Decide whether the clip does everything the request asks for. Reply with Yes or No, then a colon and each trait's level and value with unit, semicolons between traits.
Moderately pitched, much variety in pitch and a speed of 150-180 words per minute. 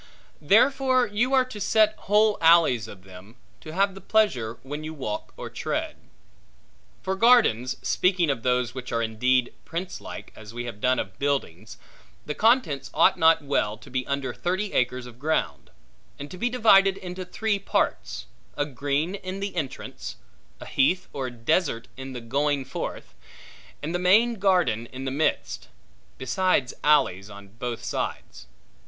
Yes: medium, 145 Hz; wide, 7.6 semitones; average, 160 wpm